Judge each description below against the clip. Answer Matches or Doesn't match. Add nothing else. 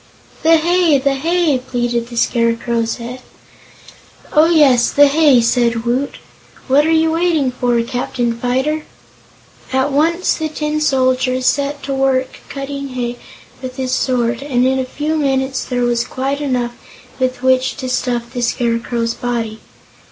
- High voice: Matches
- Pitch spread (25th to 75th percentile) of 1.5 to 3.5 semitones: Matches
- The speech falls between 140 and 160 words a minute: Matches